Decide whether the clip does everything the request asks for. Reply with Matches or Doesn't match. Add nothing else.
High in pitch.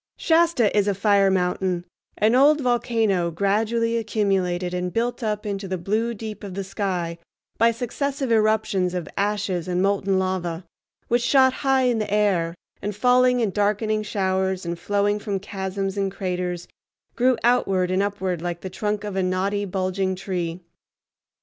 Matches